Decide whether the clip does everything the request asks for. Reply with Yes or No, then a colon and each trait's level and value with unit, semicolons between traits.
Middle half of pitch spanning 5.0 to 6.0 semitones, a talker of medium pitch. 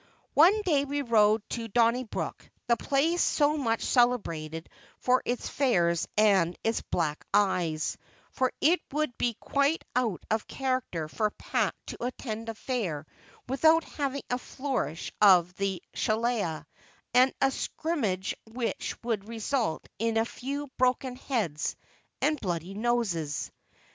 No: wide, 5.5 semitones; high, 230 Hz